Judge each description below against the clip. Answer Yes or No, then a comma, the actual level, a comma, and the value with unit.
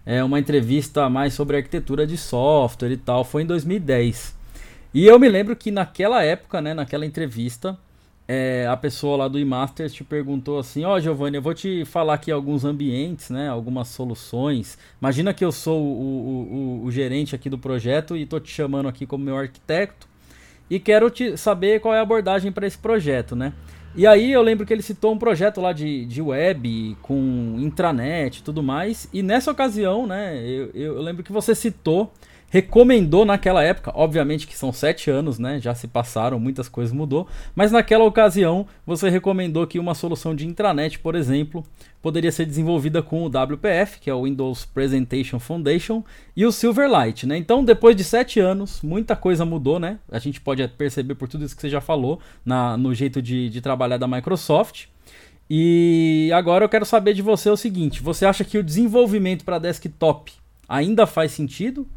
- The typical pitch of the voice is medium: Yes, medium, 155 Hz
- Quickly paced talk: Yes, fast, 190 wpm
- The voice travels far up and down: Yes, wide, 6.1 semitones